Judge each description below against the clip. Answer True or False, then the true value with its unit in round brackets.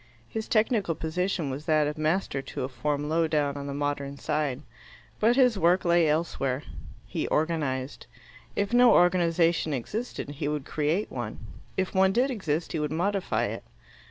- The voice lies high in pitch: False (160 Hz)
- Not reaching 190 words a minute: True (165 wpm)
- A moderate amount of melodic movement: True (4.5 semitones)